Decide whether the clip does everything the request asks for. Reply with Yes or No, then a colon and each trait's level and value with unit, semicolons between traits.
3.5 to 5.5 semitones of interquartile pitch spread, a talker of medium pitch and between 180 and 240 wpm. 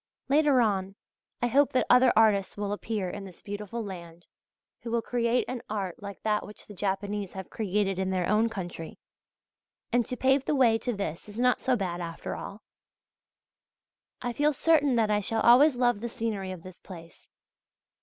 No: average, 4.1 semitones; high, 210 Hz; average, 185 wpm